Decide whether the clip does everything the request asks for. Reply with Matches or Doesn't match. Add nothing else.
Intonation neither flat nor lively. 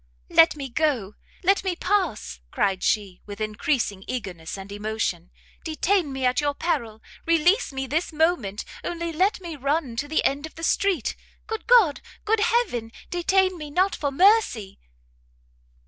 Doesn't match